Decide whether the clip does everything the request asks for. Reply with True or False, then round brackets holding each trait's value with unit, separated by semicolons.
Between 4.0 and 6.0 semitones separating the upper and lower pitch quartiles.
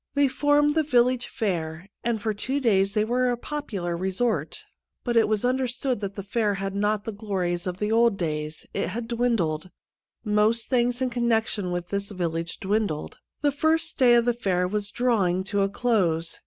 True (4.4 semitones)